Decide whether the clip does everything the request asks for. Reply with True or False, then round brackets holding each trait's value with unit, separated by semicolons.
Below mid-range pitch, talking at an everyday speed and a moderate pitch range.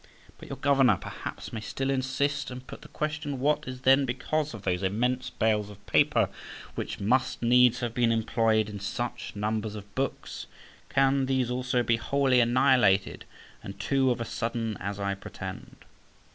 True (120 Hz; 170 wpm; 3.5 semitones)